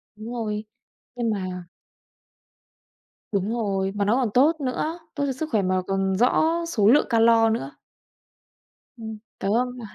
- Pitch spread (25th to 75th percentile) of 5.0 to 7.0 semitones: No, average, 3.8 semitones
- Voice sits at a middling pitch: No, high, 225 Hz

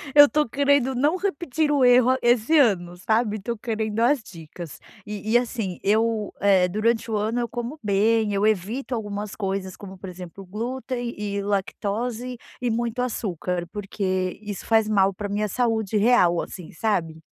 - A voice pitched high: Yes, high, 215 Hz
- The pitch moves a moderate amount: Yes, average, 3.7 semitones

